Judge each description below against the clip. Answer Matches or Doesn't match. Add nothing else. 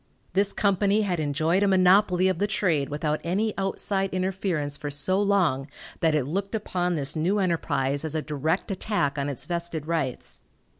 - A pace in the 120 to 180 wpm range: Matches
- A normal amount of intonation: Matches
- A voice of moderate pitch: Matches